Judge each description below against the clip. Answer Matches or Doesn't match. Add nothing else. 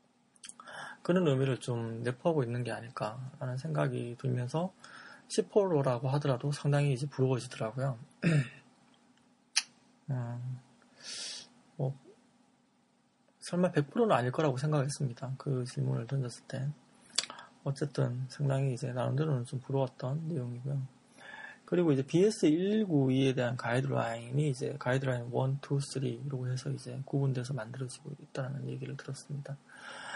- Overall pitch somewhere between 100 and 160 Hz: Matches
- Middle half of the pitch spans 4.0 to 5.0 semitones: Doesn't match